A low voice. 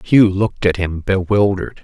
Yes: very low, 95 Hz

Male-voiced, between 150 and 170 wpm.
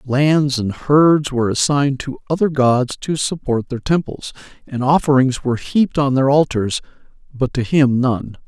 Yes: male; average, 165 wpm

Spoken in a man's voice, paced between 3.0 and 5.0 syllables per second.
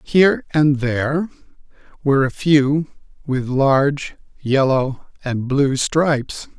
Yes: male; 3.7 syllables/s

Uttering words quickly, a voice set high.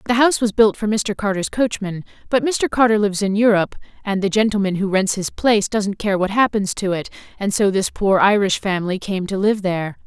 Yes: fast, 220 wpm; high, 205 Hz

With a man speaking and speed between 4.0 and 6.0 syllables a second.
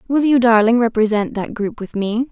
No: female; 5.2 syllables/s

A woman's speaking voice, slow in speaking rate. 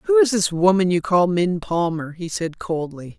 No: female; fast, 205 wpm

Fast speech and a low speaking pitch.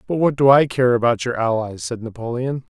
Yes: fast, 220 wpm; low, 125 Hz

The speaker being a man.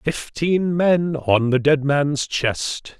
Yes: male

